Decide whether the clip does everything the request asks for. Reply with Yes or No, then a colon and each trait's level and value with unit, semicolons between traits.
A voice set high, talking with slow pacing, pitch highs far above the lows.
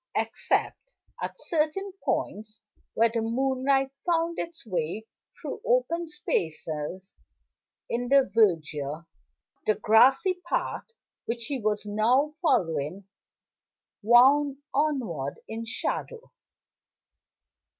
Yes: high, 235 Hz; slow, 95 wpm; wide, 6.4 semitones